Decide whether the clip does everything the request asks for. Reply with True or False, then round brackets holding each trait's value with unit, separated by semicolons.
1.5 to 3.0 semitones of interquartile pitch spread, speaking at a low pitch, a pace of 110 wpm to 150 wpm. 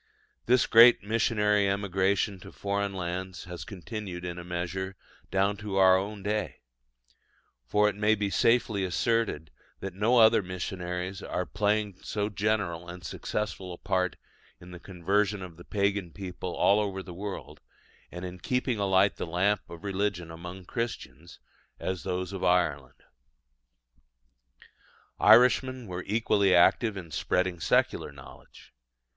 True (2.6 semitones; 95 Hz; 140 wpm)